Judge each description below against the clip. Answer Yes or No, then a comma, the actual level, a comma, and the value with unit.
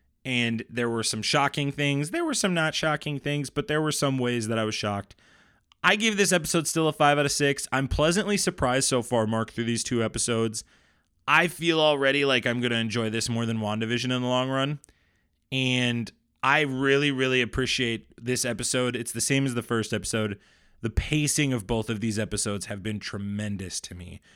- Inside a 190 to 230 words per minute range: Yes, fast, 205 wpm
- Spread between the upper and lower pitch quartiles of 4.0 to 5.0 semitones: Yes, average, 4.4 semitones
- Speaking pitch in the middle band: No, low, 120 Hz